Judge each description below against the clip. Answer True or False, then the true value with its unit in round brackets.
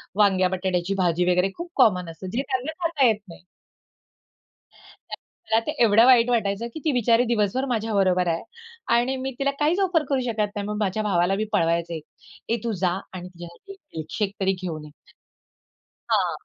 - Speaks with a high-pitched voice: True (205 Hz)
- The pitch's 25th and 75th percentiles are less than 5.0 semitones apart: False (5.3 semitones)